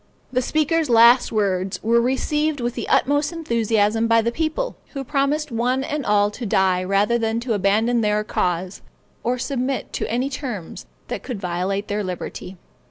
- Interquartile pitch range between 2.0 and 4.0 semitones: No, average, 4.7 semitones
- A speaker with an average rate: Yes, average, 165 wpm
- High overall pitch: Yes, high, 235 Hz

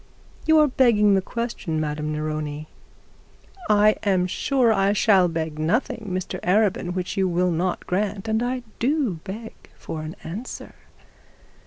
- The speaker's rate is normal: Yes, average, 150 wpm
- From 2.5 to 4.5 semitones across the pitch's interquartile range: No, average, 5.1 semitones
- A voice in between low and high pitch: No, high, 195 Hz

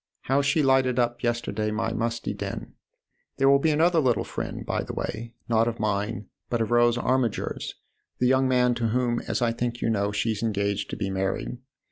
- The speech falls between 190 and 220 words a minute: Yes, average, 195 wpm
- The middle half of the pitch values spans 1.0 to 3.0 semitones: Yes, narrow, 2.4 semitones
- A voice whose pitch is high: No, low, 120 Hz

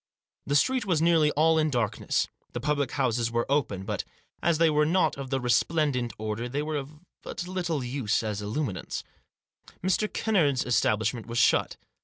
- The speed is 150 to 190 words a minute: Yes, average, 175 wpm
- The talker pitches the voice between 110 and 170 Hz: Yes, medium, 140 Hz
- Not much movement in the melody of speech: No, average, 5.0 semitones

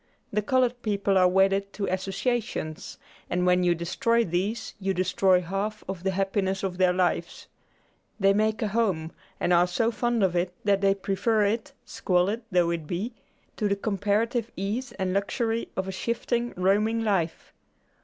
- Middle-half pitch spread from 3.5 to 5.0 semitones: No, average, 3.1 semitones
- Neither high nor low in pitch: No, high, 195 Hz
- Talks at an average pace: Yes, average, 165 wpm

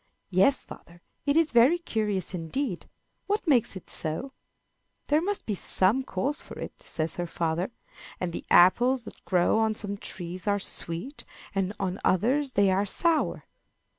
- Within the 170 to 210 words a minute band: No, average, 160 wpm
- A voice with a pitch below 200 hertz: No, high, 205 Hz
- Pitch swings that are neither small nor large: No, wide, 6.7 semitones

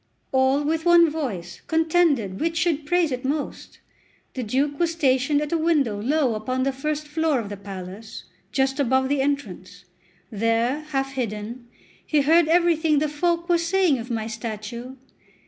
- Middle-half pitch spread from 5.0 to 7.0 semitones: Yes, wide, 5.4 semitones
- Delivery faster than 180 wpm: No, average, 165 wpm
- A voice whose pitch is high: Yes, very high, 275 Hz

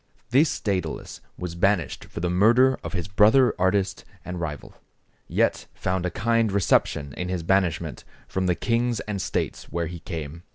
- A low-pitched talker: Yes, very low, 95 Hz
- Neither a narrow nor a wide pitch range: Yes, average, 3.6 semitones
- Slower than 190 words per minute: Yes, average, 165 wpm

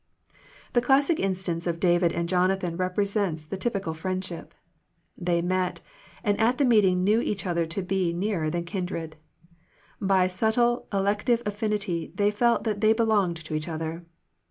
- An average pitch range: Yes, average, 3.5 semitones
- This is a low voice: No, high, 190 Hz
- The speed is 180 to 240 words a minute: No, average, 155 wpm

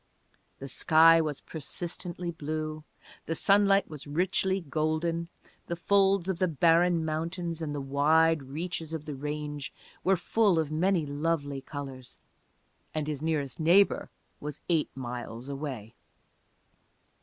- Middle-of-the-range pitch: Yes, medium, 160 Hz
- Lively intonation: No, average, 3.0 semitones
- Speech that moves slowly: Yes, slow, 130 wpm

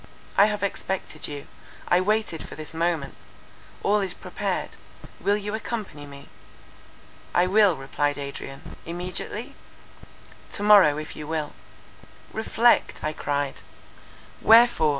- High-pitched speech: No, medium, 175 Hz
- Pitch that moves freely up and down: Yes, wide, 5.9 semitones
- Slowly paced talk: Yes, slow, 115 wpm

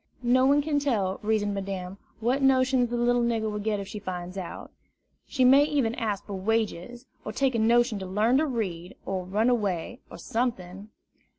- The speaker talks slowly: No, average, 195 wpm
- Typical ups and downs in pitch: Yes, average, 4.1 semitones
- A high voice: Yes, high, 220 Hz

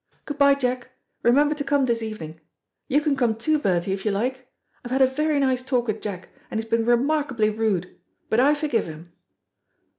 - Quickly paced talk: Yes, fast, 210 wpm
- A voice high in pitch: Yes, high, 245 Hz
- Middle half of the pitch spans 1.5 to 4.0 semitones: No, average, 4.6 semitones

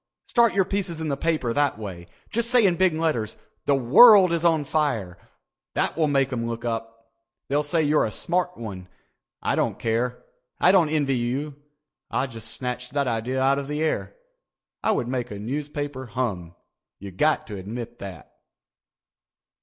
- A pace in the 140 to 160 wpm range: No, average, 175 wpm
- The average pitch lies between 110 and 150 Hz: Yes, low, 135 Hz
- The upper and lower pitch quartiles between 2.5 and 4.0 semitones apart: No, wide, 5.5 semitones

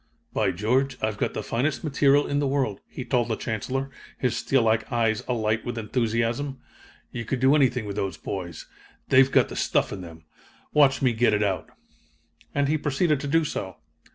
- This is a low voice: Yes, low, 125 Hz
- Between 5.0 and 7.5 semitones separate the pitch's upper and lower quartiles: No, average, 3.9 semitones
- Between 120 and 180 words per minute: No, average, 190 wpm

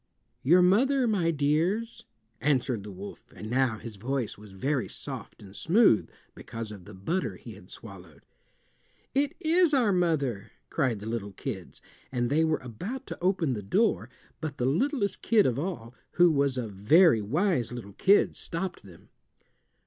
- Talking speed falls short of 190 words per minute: Yes, average, 165 wpm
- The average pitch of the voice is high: No, medium, 140 Hz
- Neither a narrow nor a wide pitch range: No, wide, 8.8 semitones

